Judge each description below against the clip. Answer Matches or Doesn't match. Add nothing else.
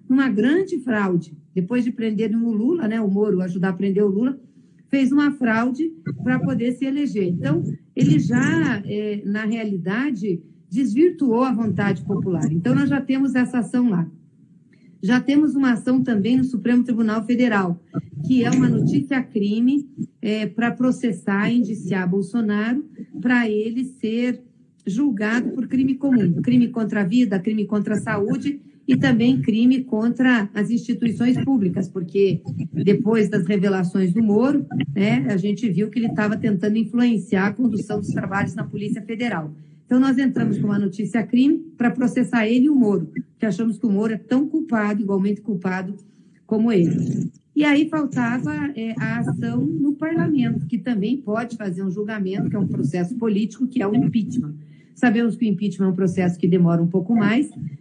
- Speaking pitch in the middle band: Doesn't match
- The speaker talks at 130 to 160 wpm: Doesn't match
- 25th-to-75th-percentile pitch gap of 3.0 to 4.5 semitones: Matches